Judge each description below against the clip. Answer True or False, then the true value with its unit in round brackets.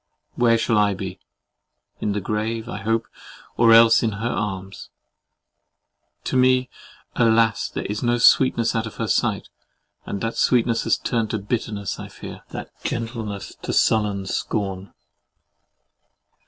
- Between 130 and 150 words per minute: True (140 wpm)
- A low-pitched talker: True (110 Hz)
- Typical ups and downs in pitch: False (2.2 semitones)